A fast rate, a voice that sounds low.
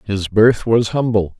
No: average, 170 wpm; low, 110 Hz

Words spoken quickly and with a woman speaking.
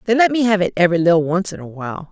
Yes: fast, 315 wpm; female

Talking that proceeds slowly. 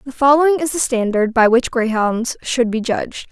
No: average, 200 wpm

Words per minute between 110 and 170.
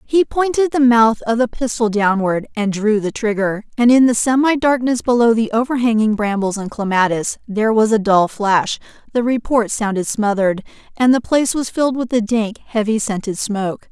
No: average, 185 wpm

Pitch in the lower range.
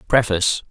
Yes: low, 105 Hz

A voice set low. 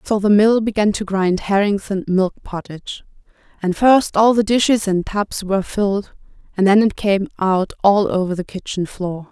No: high, 200 Hz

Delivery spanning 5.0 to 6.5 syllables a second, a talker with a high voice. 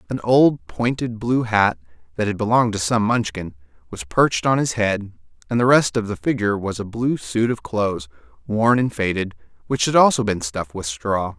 No: 5.2 syllables/s; low, 105 Hz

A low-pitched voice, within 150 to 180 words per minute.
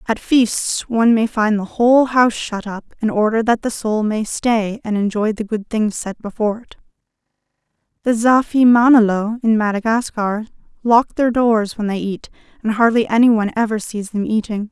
No: high, 220 Hz; average, 175 wpm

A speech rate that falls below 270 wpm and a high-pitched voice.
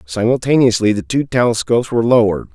No: average, 140 wpm; low, 115 Hz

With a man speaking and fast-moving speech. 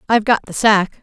No: female; fast, 235 wpm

